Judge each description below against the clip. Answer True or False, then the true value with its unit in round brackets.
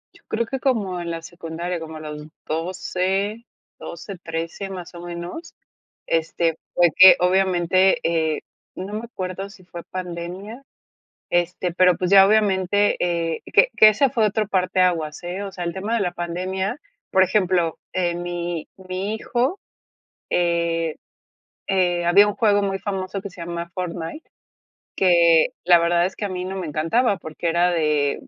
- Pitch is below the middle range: False (180 Hz)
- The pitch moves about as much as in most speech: False (2.3 semitones)